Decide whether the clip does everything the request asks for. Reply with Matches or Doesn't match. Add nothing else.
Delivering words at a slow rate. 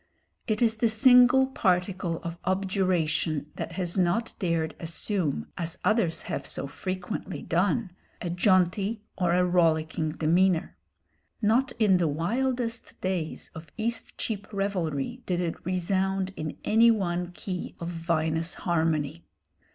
Matches